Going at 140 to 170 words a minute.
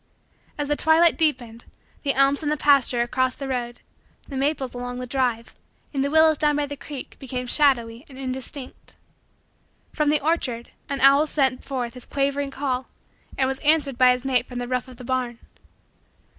No: average, 185 wpm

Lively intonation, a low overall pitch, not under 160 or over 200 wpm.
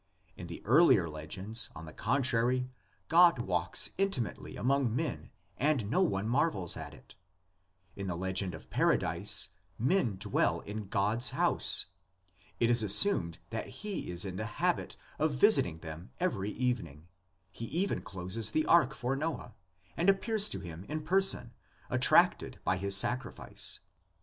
No: wide, 7.2 semitones; low, 115 Hz; average, 145 wpm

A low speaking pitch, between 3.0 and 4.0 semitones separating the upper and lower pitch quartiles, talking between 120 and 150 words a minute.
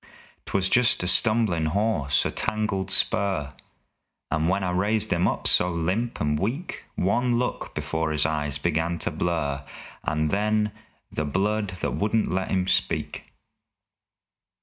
No: very low, 95 Hz; wide, 5.4 semitones; average, 145 wpm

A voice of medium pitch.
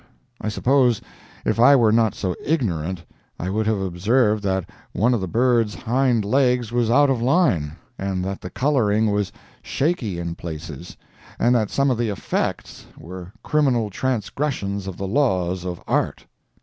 No: low, 110 Hz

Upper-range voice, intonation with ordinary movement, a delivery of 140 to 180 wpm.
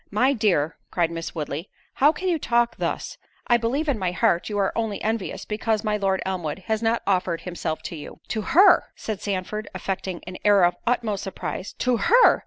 No: high, 205 Hz; average, 4.2 semitones; average, 200 wpm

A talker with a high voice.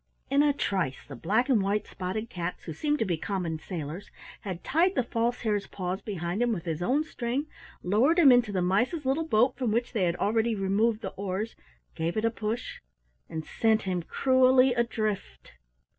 Yes: high, 215 Hz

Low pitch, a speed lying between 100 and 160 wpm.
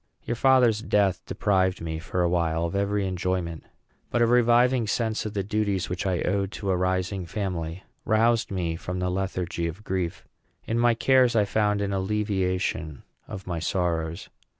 No: very low, 95 Hz; average, 175 wpm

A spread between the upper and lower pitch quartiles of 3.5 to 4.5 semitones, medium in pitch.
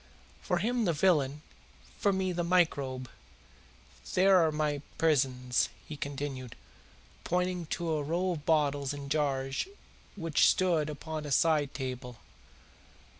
Yes: average, 3.8 semitones; medium, 150 Hz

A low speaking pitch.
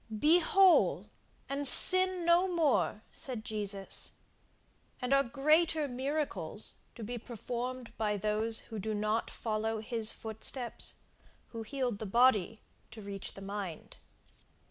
No: high, 235 Hz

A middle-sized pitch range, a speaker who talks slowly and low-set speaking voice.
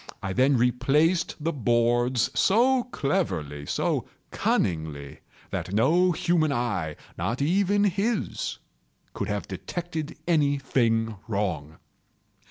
No: wide, 8.7 semitones; slow, 95 wpm; low, 130 Hz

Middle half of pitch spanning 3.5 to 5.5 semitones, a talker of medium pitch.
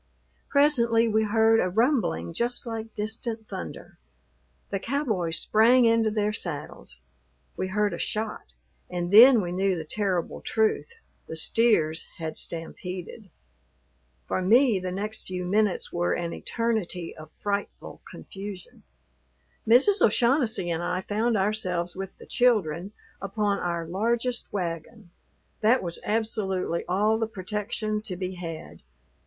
No: average, 4.0 semitones; high, 205 Hz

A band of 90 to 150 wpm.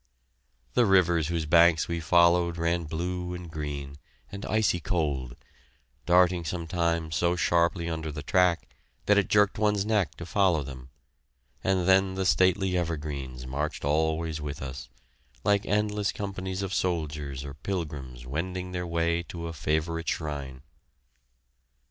Yes: average, 140 wpm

